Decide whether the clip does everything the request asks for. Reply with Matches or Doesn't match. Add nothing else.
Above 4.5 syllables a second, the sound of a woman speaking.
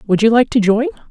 Matches